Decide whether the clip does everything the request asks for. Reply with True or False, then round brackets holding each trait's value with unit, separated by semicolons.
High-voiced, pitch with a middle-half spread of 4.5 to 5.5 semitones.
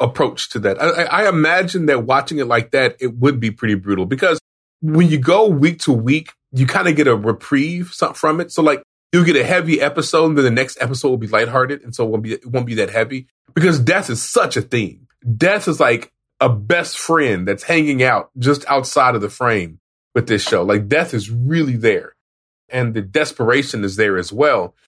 False (135 Hz; 5.2 semitones)